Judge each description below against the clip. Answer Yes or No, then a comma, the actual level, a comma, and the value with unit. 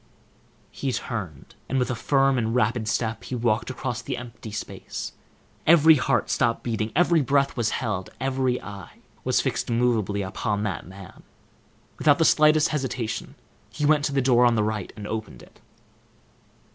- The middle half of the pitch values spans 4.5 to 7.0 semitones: No, average, 3.8 semitones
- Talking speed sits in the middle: Yes, average, 165 wpm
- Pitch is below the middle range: Yes, low, 120 Hz